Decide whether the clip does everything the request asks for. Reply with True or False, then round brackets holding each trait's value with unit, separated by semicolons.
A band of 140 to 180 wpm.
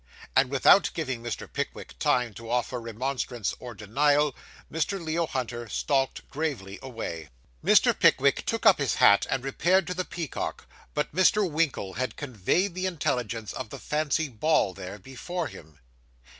True (155 wpm)